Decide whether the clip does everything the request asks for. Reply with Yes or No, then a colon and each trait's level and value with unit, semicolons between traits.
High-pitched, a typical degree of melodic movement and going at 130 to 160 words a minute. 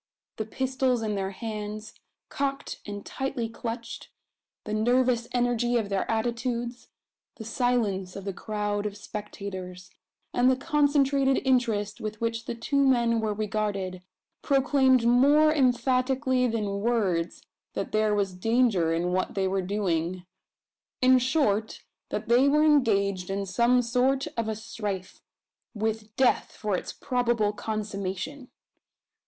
Yes: high, 225 Hz; average, 3.7 semitones; slow, 135 wpm